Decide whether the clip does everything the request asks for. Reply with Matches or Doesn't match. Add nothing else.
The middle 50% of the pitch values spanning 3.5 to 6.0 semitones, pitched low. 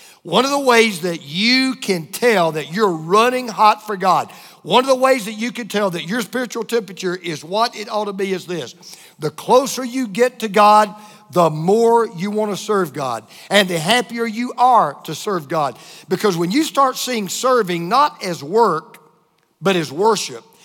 Doesn't match